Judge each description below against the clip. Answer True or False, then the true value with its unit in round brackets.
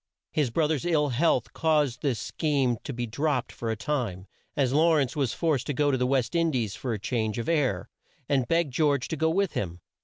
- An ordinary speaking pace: False (220 wpm)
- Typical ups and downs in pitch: True (4.3 semitones)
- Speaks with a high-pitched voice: False (140 Hz)